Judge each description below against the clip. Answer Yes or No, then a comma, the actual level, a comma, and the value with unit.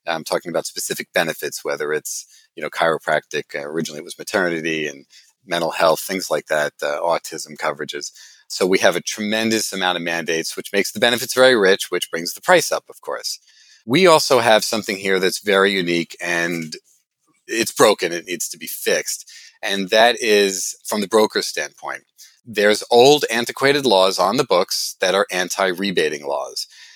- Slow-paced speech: No, average, 175 wpm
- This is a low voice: Yes, low, 110 Hz